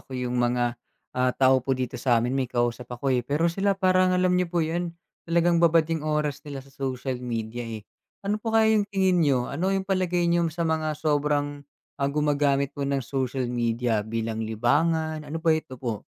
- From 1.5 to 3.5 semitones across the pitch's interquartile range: No, average, 5.2 semitones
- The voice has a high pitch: No, medium, 145 Hz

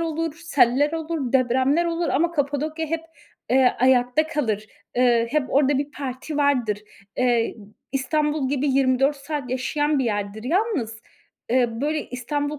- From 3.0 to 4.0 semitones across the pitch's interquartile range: Yes, average, 3.3 semitones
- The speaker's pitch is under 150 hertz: No, very high, 275 Hz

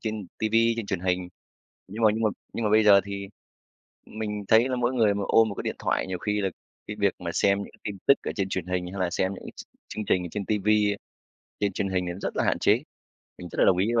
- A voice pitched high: No, low, 100 Hz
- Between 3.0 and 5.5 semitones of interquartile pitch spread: No, narrow, 2.4 semitones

